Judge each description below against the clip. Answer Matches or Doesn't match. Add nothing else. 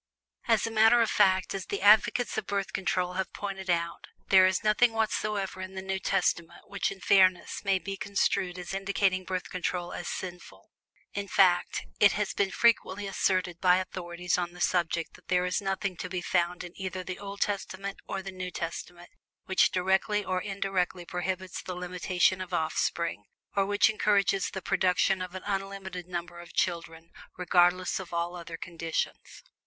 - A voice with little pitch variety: Matches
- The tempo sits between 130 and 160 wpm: Doesn't match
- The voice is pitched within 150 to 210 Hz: Matches